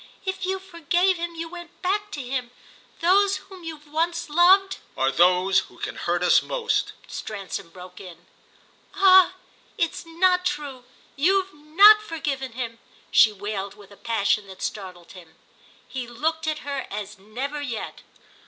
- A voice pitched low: No, very high, 295 Hz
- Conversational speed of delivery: Yes, average, 150 wpm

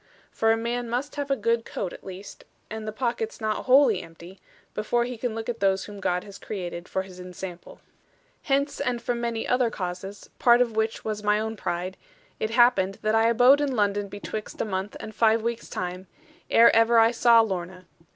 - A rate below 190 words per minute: No, average, 200 wpm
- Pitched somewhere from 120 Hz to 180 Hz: No, high, 220 Hz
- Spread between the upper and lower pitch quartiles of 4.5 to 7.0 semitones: No, average, 3.6 semitones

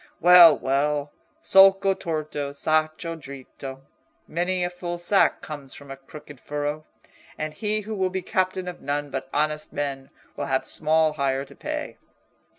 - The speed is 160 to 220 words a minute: No, average, 150 wpm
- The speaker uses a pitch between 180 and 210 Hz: No, medium, 155 Hz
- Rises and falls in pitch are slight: No, average, 3.8 semitones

